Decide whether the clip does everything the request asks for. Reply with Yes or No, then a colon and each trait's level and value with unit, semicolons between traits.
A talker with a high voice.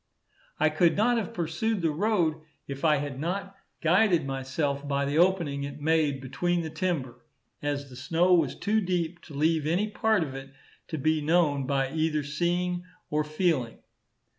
No: medium, 160 Hz